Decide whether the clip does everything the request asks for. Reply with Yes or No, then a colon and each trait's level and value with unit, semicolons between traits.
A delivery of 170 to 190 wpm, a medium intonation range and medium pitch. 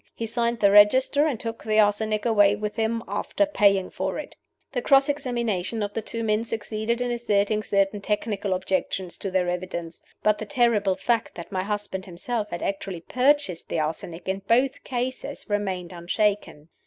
No: average, 175 wpm; average, 3.4 semitones; high, 210 Hz